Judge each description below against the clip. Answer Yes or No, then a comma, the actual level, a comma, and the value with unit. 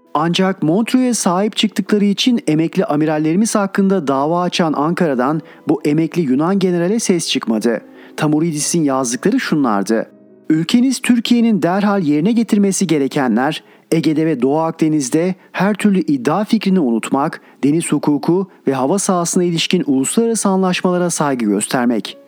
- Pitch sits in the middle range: Yes, medium, 170 Hz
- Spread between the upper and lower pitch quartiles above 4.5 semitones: Yes, average, 5.0 semitones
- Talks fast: No, average, 120 wpm